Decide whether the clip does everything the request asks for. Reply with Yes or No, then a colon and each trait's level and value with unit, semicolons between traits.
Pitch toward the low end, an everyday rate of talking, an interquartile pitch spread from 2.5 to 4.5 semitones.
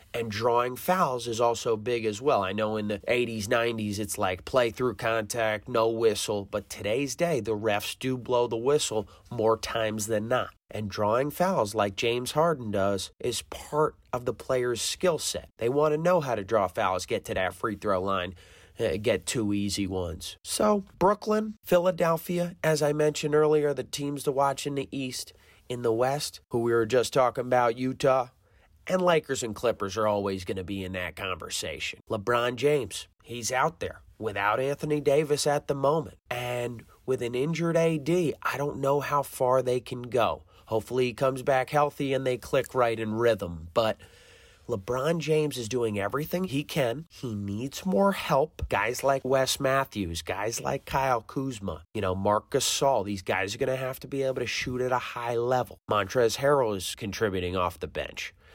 No: low, 120 Hz; average, 190 wpm; average, 5.1 semitones